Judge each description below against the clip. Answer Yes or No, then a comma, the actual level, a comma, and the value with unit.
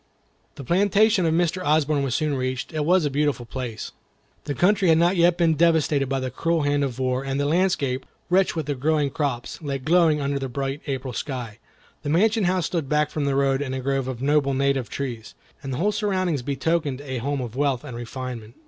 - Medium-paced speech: No, fast, 215 wpm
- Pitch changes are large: No, average, 3.9 semitones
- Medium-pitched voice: Yes, medium, 145 Hz